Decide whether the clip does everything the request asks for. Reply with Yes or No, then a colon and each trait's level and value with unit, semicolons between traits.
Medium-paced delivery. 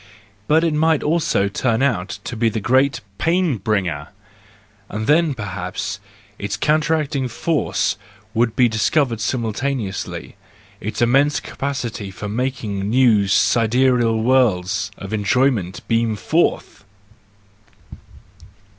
No: slow, 110 wpm